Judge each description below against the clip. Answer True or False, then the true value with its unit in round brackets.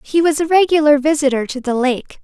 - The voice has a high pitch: True (290 Hz)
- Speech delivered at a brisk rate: True (215 wpm)